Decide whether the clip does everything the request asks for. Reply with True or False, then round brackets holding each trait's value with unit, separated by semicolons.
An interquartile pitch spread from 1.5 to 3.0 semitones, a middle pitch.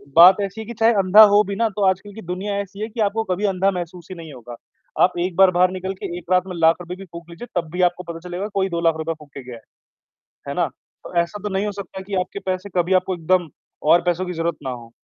True (2.5 semitones; 180 Hz)